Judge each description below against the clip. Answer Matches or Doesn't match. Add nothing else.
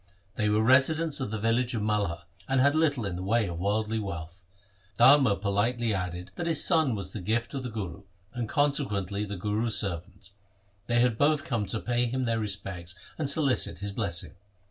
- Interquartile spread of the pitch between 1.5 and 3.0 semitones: Doesn't match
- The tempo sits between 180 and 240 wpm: Matches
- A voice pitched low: Matches